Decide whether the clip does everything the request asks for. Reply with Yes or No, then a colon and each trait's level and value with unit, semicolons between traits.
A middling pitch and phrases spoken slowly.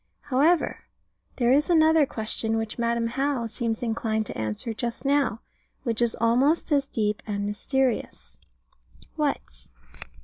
No: high, 235 Hz; slow, 130 wpm